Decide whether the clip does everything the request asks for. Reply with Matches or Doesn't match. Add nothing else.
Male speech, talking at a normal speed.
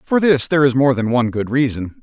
Doesn't match